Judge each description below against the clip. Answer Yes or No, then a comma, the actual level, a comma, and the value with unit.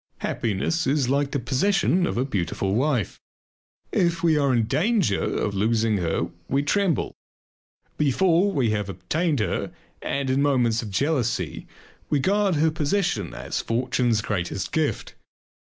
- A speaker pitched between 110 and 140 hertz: Yes, low, 135 Hz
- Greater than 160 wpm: No, average, 140 wpm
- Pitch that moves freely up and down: Yes, wide, 6.3 semitones